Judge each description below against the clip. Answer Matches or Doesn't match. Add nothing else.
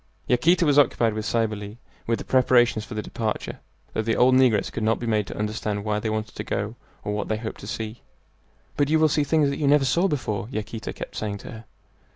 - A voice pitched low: Matches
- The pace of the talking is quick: Matches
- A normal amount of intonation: Matches